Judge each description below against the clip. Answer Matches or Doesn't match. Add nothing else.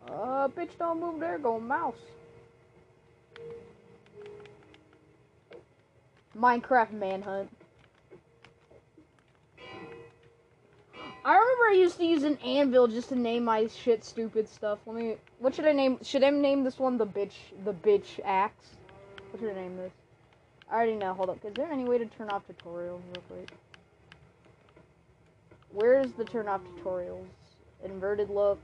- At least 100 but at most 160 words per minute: Matches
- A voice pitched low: Doesn't match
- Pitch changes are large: Matches